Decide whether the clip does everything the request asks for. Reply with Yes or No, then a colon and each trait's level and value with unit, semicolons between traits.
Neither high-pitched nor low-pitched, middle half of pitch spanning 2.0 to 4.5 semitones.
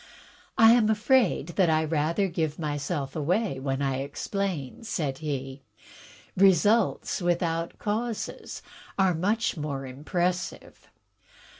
No: medium, 170 Hz; wide, 5.4 semitones